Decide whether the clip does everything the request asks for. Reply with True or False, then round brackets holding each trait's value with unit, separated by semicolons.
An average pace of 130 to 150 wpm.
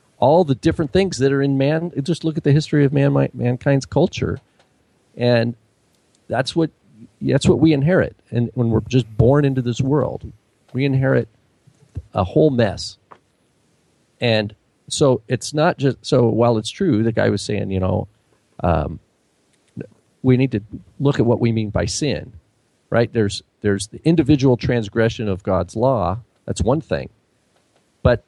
False (160 wpm)